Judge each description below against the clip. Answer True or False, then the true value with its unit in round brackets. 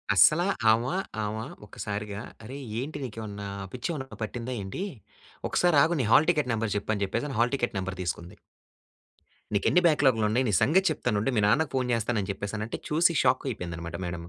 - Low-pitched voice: True (115 Hz)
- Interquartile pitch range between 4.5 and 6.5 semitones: True (4.9 semitones)